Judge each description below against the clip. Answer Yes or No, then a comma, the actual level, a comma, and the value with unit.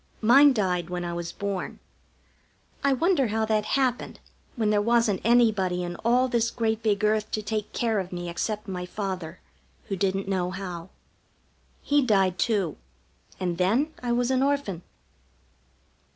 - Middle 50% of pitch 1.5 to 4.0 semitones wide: No, average, 4.4 semitones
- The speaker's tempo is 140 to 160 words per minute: Yes, average, 155 wpm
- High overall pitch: Yes, high, 210 Hz